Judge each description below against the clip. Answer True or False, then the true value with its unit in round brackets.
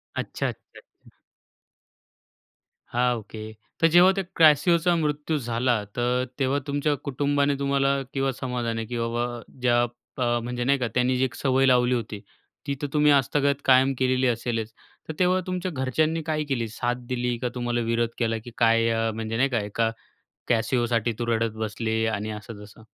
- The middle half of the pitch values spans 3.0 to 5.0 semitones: True (3.4 semitones)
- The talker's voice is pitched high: False (125 Hz)